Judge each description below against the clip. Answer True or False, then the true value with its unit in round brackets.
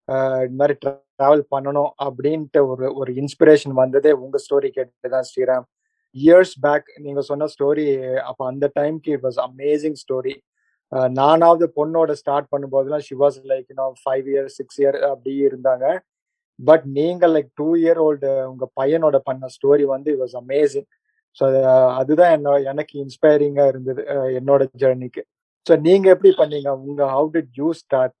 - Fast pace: True (140 wpm)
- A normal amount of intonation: False (2.2 semitones)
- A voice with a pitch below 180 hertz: True (140 Hz)